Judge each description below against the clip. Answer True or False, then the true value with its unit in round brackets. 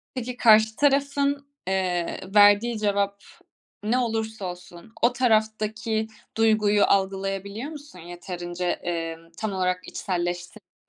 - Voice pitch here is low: False (205 Hz)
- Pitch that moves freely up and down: False (3.6 semitones)